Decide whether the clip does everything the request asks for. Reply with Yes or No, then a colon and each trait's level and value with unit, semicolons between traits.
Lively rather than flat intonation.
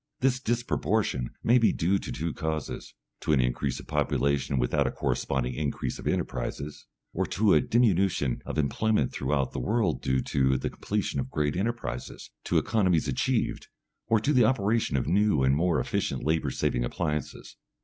Yes: wide, 8.2 semitones